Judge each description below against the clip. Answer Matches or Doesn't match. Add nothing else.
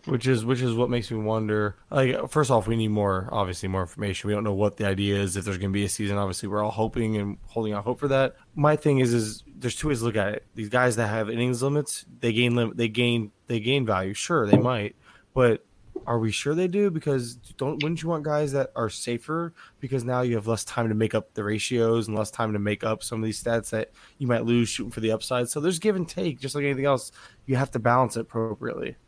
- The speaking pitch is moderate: Doesn't match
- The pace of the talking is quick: Matches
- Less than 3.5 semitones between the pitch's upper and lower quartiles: Doesn't match